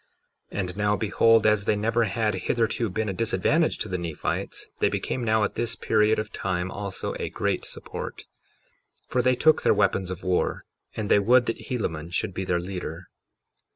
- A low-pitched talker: Yes, low, 105 Hz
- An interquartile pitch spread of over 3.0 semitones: Yes, average, 3.5 semitones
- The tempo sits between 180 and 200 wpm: Yes, average, 190 wpm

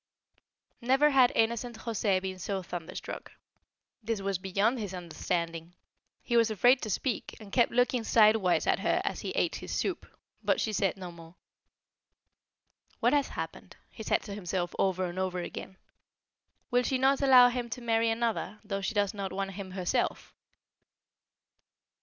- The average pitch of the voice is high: Yes, high, 210 Hz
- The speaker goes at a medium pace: Yes, average, 160 wpm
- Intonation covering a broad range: No, average, 4.1 semitones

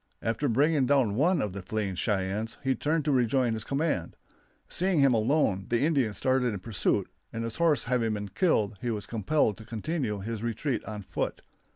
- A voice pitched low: Yes, low, 115 Hz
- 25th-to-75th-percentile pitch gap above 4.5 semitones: Yes, average, 4.9 semitones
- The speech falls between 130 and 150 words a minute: No, average, 190 wpm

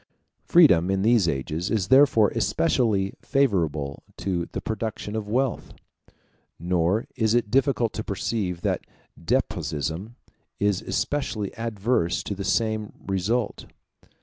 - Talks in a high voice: No, low, 105 Hz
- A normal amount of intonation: Yes, average, 4.1 semitones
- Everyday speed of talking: No, slow, 120 wpm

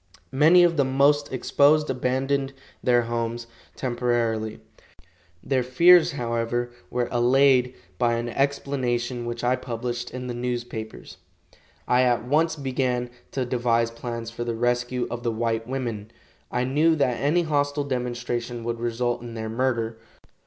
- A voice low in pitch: Yes, low, 125 Hz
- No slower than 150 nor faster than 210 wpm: No, average, 140 wpm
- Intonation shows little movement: Yes, narrow, 2.2 semitones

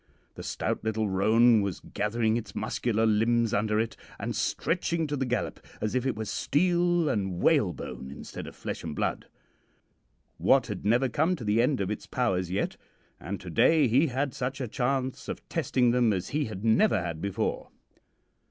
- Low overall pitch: Yes, low, 115 Hz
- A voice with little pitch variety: No, average, 4.2 semitones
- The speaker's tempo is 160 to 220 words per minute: Yes, average, 185 wpm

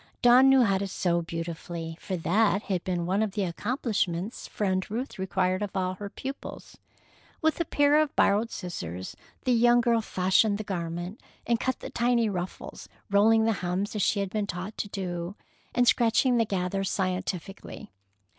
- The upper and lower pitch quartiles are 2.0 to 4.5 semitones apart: Yes, average, 3.9 semitones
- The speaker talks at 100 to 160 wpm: No, average, 175 wpm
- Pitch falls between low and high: No, high, 200 Hz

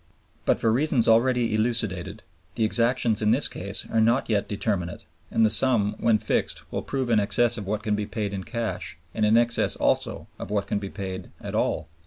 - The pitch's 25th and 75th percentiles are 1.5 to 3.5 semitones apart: Yes, narrow, 2.4 semitones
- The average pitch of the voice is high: No, low, 110 Hz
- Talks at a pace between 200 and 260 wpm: Yes, fast, 205 wpm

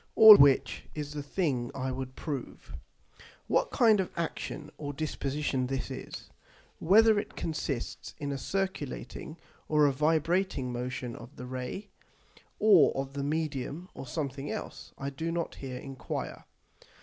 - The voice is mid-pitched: Yes, medium, 145 Hz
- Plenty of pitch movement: No, average, 4.0 semitones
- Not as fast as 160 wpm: Yes, average, 145 wpm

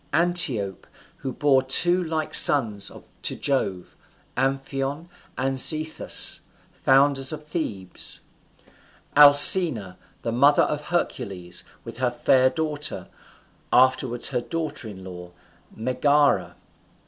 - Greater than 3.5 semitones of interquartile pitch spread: Yes, average, 4.3 semitones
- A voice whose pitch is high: No, low, 135 Hz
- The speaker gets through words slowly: Yes, slow, 100 wpm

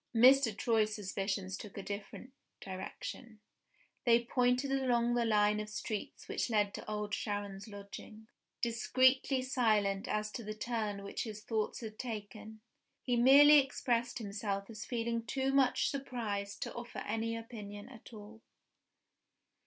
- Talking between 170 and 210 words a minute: No, average, 140 wpm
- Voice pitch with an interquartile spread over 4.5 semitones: No, average, 2.8 semitones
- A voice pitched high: Yes, high, 220 Hz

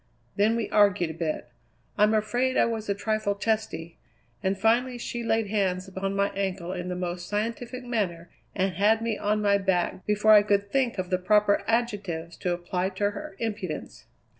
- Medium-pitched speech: No, high, 205 Hz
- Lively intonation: No, average, 3.0 semitones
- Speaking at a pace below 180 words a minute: No, average, 185 wpm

